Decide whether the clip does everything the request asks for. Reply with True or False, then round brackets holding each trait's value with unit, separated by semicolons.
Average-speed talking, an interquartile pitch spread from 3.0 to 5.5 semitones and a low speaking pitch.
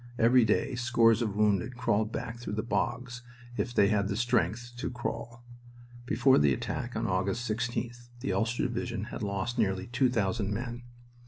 False (170 wpm; 2.4 semitones; 115 Hz)